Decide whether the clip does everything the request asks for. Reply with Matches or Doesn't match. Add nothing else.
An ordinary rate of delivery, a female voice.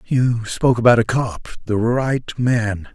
Doesn't match